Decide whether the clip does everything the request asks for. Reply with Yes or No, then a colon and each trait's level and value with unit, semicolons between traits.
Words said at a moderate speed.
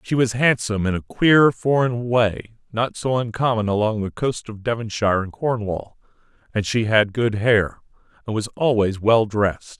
Yes: average, 170 wpm